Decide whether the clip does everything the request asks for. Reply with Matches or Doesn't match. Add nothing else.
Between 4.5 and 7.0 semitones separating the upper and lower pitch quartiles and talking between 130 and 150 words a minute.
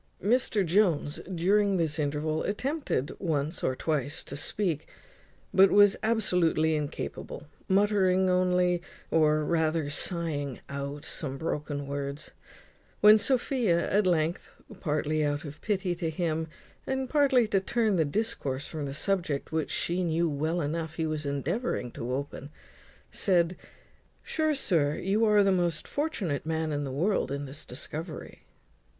Matches